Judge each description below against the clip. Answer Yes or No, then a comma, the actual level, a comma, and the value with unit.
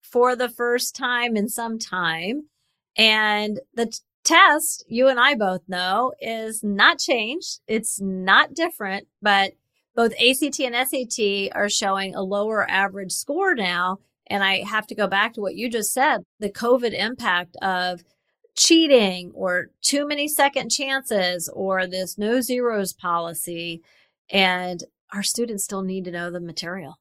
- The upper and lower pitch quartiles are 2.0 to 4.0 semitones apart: No, average, 4.8 semitones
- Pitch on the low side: No, high, 210 Hz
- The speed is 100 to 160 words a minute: Yes, average, 155 wpm